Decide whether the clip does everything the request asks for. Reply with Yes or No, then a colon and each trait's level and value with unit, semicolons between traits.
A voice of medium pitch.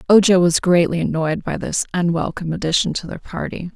Yes: medium, 175 Hz